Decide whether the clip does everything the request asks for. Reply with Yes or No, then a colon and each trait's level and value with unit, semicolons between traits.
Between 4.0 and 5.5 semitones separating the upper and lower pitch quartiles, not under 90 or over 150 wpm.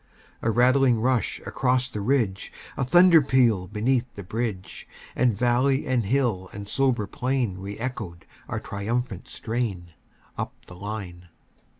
Yes: average, 4.4 semitones; slow, 135 wpm